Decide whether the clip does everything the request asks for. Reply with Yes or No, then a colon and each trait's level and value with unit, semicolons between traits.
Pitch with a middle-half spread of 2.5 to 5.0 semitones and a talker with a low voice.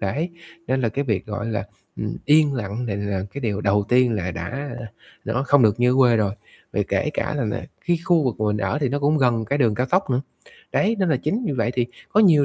No: wide, 5.4 semitones; low, 125 Hz